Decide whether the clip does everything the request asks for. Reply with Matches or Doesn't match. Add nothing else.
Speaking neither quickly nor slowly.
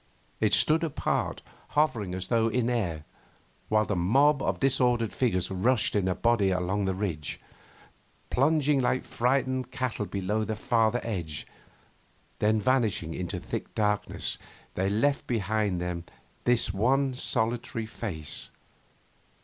Doesn't match